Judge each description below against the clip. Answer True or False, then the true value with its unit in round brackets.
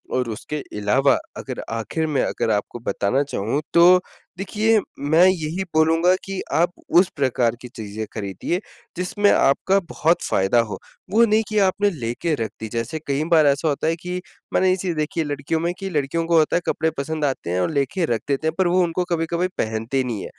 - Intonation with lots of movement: True (6.1 semitones)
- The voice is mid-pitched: True (155 Hz)